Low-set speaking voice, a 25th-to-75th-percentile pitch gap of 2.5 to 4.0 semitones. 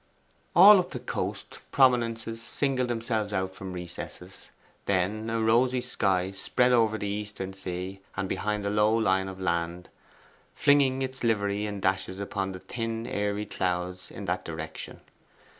Yes: low, 105 Hz; average, 3.5 semitones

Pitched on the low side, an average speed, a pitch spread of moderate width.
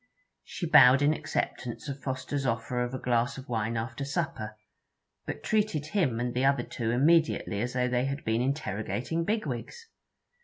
Yes: low, 130 Hz; average, 165 wpm; average, 3.8 semitones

